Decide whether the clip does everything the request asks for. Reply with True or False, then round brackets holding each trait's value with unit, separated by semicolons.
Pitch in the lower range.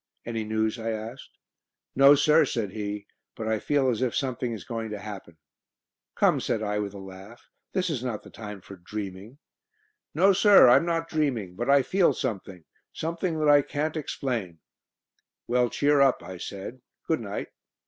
True (115 Hz)